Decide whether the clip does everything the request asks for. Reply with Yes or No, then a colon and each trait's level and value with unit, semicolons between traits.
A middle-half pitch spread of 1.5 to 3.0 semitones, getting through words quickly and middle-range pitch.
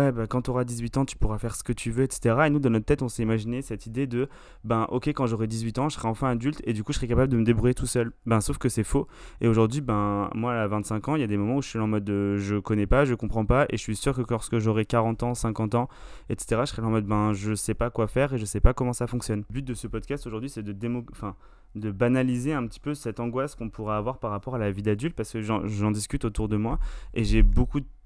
No: average, 2.7 semitones; fast, 300 wpm; low, 115 Hz